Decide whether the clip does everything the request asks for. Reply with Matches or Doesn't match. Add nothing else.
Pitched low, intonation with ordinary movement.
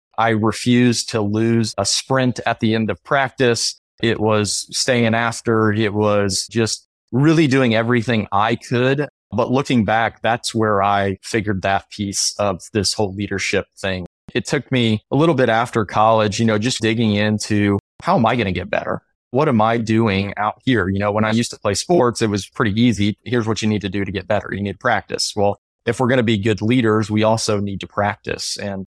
Doesn't match